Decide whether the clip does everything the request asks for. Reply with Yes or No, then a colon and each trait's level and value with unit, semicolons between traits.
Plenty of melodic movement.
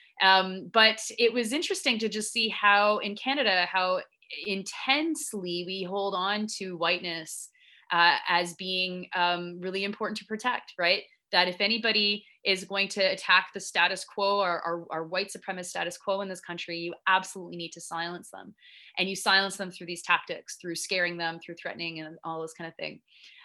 No: average, 3.2 semitones